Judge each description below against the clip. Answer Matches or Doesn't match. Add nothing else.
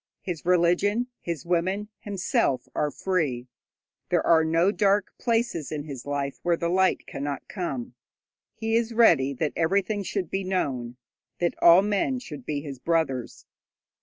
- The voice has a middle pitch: Matches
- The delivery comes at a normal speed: Matches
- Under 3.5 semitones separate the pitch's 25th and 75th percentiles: Doesn't match